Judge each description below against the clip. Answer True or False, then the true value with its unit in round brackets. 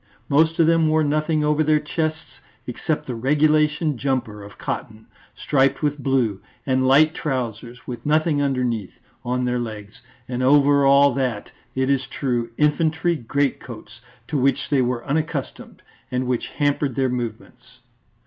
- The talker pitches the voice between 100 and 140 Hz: True (135 Hz)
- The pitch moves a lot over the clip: False (3.5 semitones)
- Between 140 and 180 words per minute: True (150 wpm)